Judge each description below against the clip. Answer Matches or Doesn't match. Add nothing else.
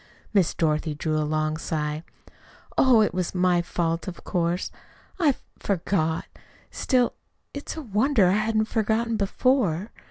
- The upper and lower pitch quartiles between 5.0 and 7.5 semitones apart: Matches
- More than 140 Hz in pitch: Matches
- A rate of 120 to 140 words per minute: Matches